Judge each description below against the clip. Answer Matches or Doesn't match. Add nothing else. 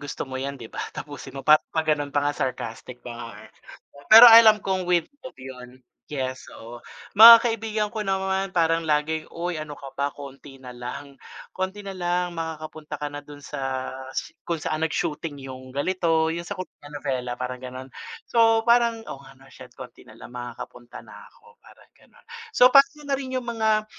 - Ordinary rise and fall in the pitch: Doesn't match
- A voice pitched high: Doesn't match